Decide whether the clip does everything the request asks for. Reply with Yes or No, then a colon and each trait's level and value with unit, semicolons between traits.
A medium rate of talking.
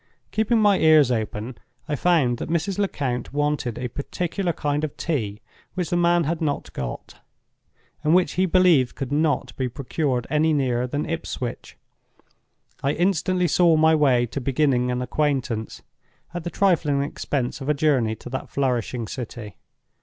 Yes: average, 160 wpm